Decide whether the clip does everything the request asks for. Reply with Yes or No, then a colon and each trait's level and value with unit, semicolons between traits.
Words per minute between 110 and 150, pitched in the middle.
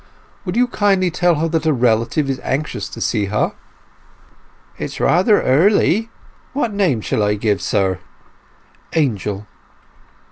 Yes: average, 140 wpm; medium, 150 Hz